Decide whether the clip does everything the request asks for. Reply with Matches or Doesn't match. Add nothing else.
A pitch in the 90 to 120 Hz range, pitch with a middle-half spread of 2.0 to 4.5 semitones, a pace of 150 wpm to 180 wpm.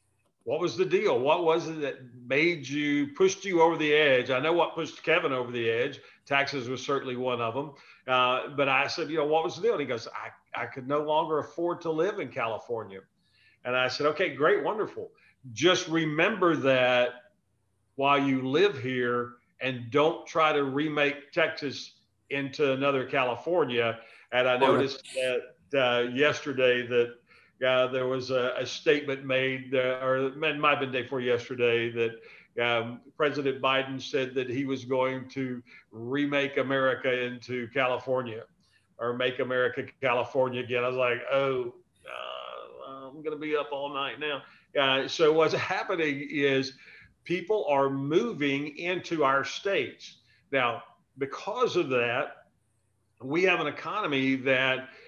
Doesn't match